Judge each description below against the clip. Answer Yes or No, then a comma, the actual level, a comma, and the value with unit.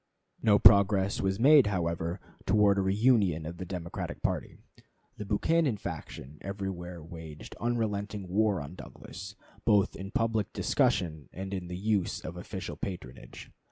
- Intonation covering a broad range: No, average, 3.1 semitones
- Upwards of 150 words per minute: No, average, 140 wpm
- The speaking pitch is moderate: No, very low, 95 Hz